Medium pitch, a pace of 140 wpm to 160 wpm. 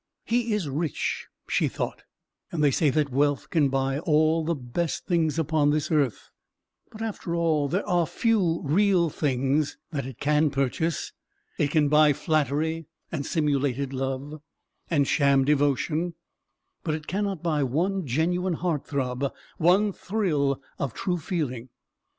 Yes: medium, 155 Hz; average, 145 wpm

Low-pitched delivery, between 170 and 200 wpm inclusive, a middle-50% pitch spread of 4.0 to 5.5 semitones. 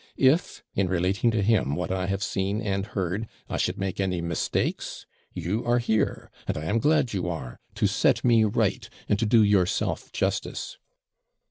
No: low, 100 Hz; average, 175 wpm; average, 3.5 semitones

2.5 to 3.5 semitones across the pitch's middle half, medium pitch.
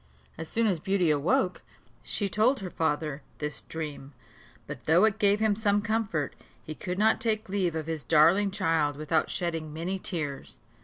No: average, 4.6 semitones; medium, 175 Hz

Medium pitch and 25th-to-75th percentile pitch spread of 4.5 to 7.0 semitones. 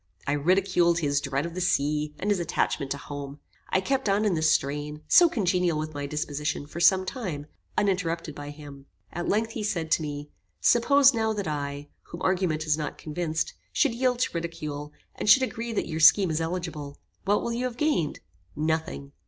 Yes: medium, 165 Hz; average, 5.0 semitones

